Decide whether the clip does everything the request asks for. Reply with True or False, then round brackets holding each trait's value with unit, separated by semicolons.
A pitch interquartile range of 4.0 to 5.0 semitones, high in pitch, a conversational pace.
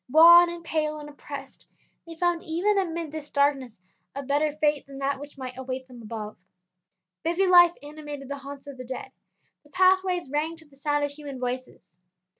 False (3.3 semitones; 290 Hz; 185 wpm)